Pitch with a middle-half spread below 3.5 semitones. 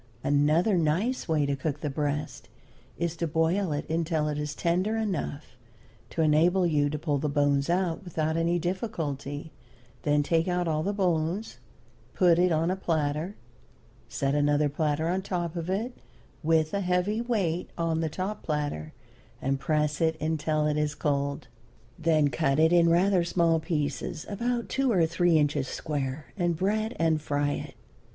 Yes: average, 3.1 semitones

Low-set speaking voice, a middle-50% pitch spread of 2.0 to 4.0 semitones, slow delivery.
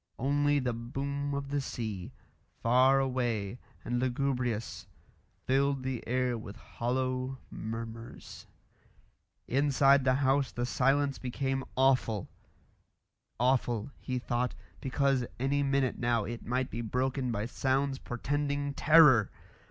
Yes: low, 130 Hz; narrow, 2.4 semitones; slow, 115 wpm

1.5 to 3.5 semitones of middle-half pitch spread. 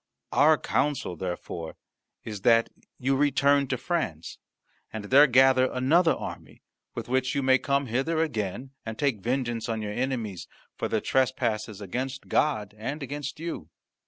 No: average, 4.2 semitones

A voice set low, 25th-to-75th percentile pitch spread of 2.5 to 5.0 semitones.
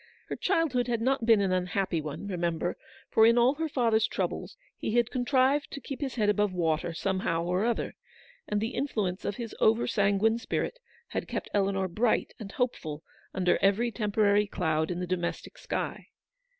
No: high, 210 Hz; average, 4.7 semitones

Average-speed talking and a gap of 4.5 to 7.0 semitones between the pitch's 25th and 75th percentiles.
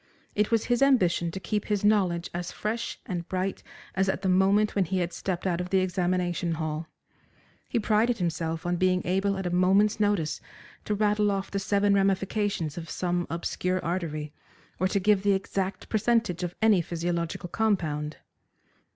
No: average, 175 wpm; average, 2.9 semitones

